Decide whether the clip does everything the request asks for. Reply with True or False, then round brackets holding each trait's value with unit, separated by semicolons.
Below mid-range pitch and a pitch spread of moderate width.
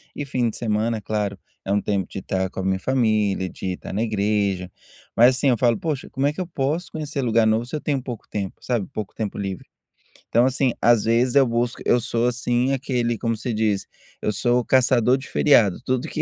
True (115 Hz; 3.7 semitones)